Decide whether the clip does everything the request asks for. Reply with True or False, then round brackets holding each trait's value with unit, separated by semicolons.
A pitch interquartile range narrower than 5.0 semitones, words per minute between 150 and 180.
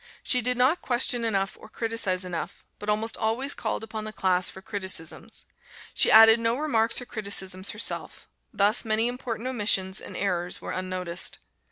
True (3.5 semitones; 165 wpm)